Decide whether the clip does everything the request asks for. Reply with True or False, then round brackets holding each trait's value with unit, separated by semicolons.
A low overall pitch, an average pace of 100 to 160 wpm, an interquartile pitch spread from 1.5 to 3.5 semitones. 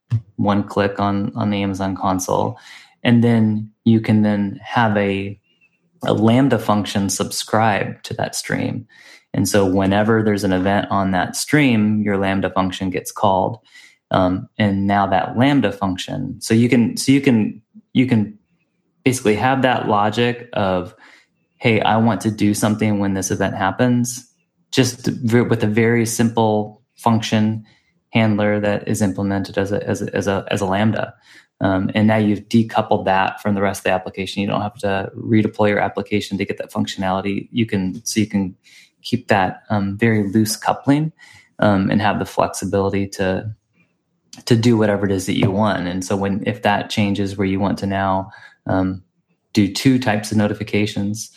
False (105 Hz; 175 wpm; 2.7 semitones)